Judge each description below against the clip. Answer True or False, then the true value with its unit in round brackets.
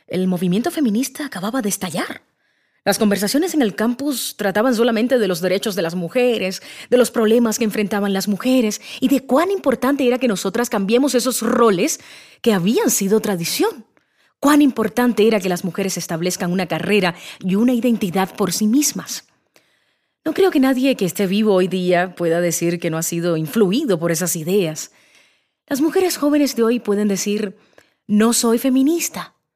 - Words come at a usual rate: True (170 wpm)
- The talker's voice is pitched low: False (220 Hz)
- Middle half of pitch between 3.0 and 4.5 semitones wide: False (5.2 semitones)